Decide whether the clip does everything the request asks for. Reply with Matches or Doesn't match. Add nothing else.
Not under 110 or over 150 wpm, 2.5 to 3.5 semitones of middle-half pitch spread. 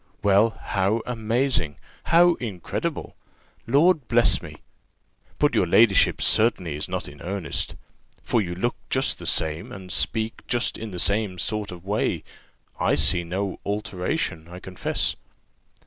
Doesn't match